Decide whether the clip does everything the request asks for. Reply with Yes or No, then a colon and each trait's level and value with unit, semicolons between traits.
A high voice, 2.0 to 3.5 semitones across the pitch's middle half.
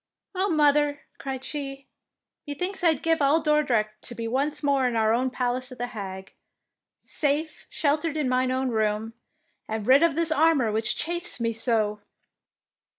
No: very high, 265 Hz; average, 4.7 semitones